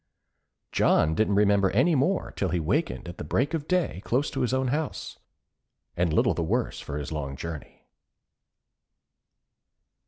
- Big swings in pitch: Yes, wide, 9.0 semitones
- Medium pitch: No, low, 105 Hz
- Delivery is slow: No, average, 155 wpm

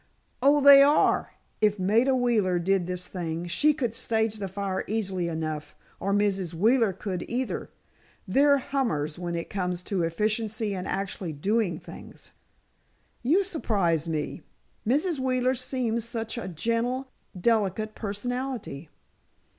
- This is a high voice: Yes, high, 210 Hz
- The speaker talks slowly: Yes, slow, 130 wpm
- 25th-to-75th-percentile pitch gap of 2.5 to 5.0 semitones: No, wide, 5.4 semitones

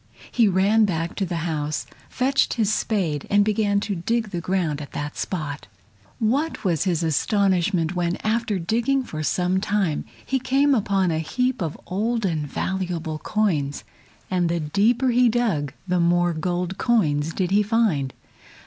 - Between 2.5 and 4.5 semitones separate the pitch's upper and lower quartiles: No, average, 4.9 semitones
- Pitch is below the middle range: No, medium, 185 Hz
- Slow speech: No, average, 160 wpm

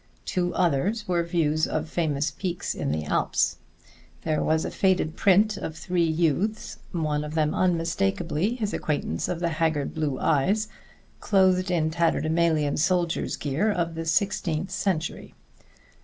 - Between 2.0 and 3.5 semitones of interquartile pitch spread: Yes, average, 2.8 semitones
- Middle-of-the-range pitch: Yes, medium, 165 Hz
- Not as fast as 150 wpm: Yes, average, 140 wpm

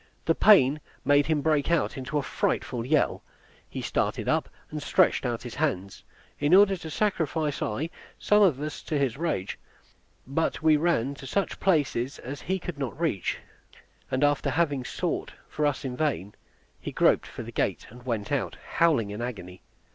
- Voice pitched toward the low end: No, medium, 145 Hz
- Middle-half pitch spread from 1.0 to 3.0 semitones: No, average, 4.2 semitones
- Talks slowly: No, average, 180 wpm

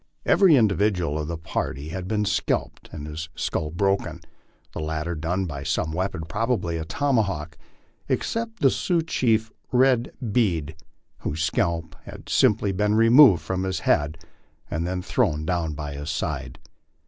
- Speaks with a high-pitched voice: No, very low, 90 Hz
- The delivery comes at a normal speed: Yes, average, 155 wpm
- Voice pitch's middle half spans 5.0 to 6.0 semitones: Yes, wide, 5.5 semitones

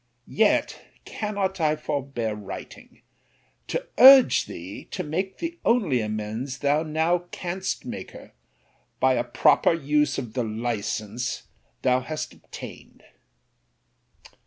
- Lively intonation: Yes, wide, 6.7 semitones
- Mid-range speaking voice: Yes, medium, 145 Hz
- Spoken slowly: Yes, slow, 115 wpm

